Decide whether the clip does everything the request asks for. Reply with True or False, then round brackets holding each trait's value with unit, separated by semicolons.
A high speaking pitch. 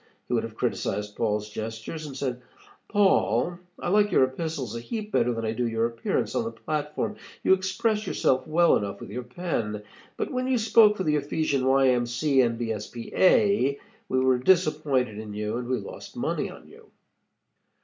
False (130 Hz)